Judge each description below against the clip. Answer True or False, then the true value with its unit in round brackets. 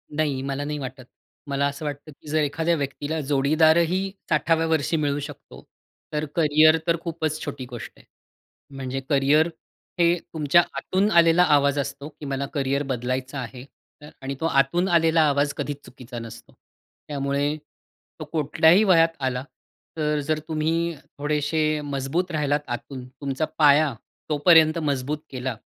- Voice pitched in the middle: True (145 Hz)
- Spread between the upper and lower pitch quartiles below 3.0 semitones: True (2.6 semitones)